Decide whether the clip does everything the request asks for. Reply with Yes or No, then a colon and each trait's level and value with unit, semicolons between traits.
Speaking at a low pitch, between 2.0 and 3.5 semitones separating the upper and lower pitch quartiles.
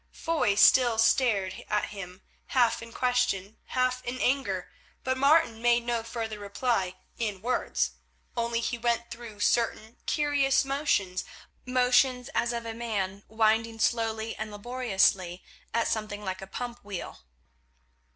No: high, 230 Hz; average, 3.2 semitones